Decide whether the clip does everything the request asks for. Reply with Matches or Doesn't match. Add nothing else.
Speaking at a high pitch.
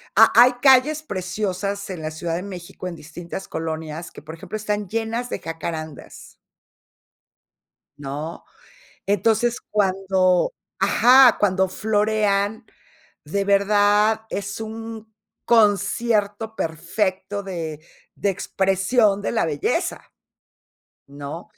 Matches